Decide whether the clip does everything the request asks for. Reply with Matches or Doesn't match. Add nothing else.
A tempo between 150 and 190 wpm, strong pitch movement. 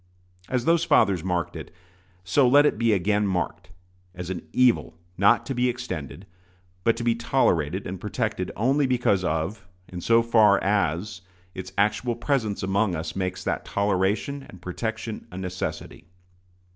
Doesn't match